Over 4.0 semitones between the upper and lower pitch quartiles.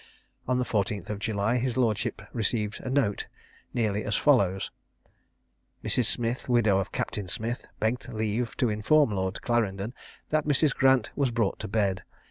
No: average, 3.5 semitones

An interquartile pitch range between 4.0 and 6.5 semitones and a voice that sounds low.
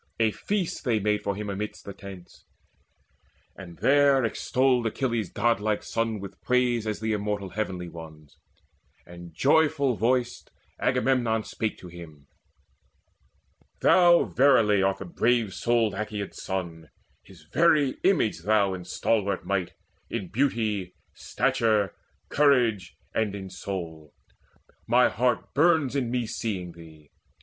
Yes: average, 4.7 semitones; low, 105 Hz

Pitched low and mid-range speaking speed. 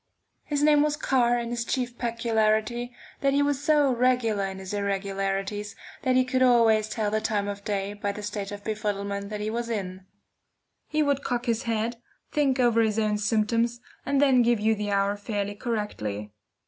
No: high, 220 Hz; average, 185 wpm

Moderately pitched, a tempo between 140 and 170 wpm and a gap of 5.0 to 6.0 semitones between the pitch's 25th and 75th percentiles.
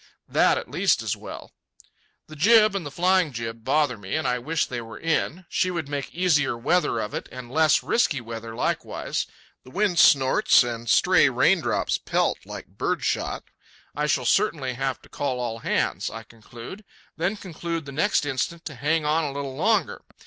No: medium, 145 Hz; average, 180 wpm; wide, 5.5 semitones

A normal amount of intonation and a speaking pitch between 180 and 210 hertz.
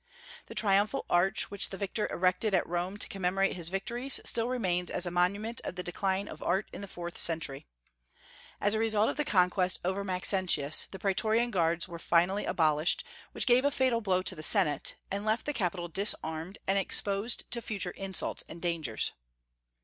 Yes: average, 3.2 semitones; high, 190 Hz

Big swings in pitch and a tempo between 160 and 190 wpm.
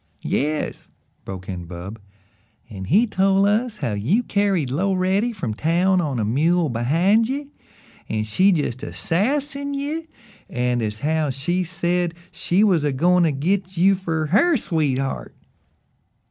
No: wide, 6.8 semitones; average, 145 wpm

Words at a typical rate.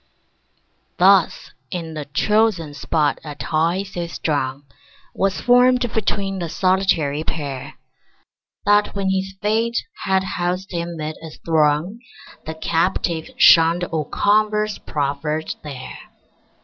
No: slow, 115 wpm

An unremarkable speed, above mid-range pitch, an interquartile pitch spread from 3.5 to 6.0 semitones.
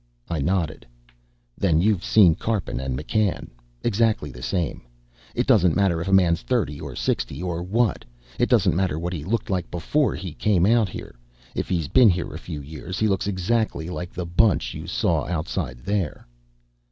No: average, 180 wpm; very low, 90 Hz; average, 4.0 semitones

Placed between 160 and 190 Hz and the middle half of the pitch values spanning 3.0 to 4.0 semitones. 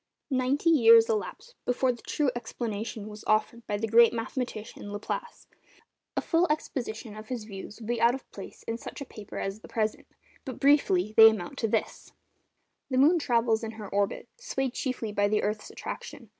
No: high, 230 Hz; average, 3.3 semitones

